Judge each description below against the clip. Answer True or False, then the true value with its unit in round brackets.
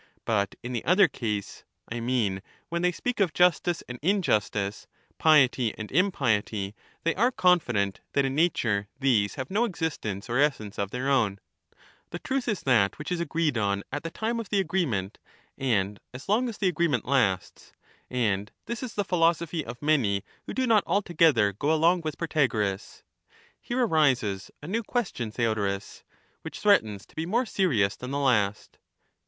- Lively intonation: True (8.9 semitones)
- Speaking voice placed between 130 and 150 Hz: True (135 Hz)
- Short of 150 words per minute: False (170 wpm)